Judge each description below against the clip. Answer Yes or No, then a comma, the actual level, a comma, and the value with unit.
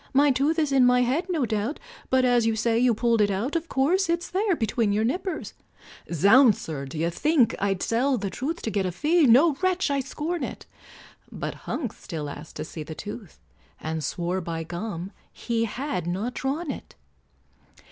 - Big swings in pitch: Yes, wide, 7.0 semitones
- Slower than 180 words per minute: No, average, 190 wpm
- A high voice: Yes, high, 240 Hz